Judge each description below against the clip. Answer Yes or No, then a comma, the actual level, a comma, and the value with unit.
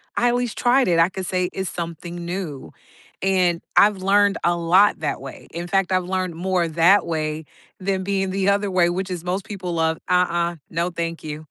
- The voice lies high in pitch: No, medium, 180 Hz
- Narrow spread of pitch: Yes, narrow, 2.2 semitones